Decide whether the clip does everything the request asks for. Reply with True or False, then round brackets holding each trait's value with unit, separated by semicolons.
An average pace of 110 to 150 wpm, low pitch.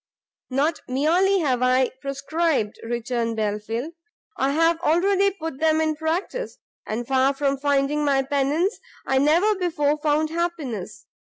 False (135 wpm; 290 Hz)